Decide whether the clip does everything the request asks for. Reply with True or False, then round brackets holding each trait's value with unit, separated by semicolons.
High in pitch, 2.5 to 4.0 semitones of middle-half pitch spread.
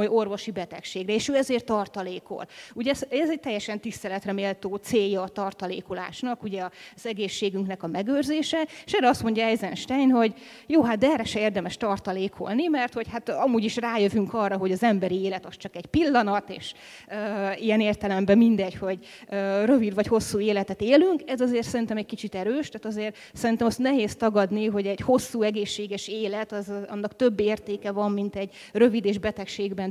True (210 Hz; 2.8 semitones)